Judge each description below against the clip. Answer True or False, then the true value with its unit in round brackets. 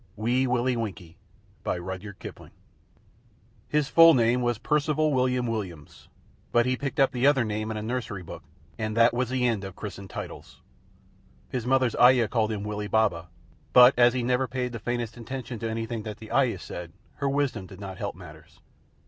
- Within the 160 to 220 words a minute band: True (195 wpm)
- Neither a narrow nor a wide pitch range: True (3.4 semitones)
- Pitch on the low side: True (120 Hz)